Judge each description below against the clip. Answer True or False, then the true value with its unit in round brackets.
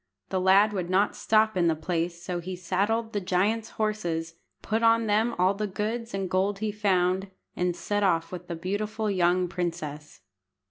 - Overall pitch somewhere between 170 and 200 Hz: True (190 Hz)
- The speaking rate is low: False (180 wpm)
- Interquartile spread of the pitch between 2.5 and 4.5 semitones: True (3.1 semitones)